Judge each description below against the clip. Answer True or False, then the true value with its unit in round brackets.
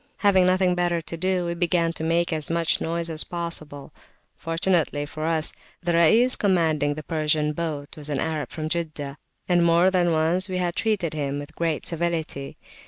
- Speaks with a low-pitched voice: False (165 Hz)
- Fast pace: False (180 wpm)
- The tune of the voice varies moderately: False (2.1 semitones)